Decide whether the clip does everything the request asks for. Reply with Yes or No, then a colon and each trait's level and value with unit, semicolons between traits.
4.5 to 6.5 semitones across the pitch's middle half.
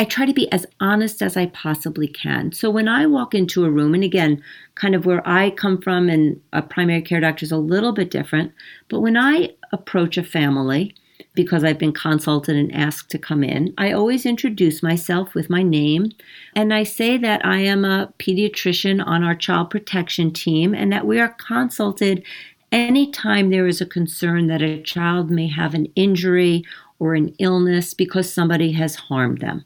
No: average, 3.8 semitones